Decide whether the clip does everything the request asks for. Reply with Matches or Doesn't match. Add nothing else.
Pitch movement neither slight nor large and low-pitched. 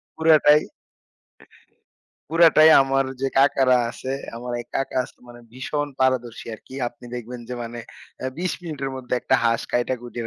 Matches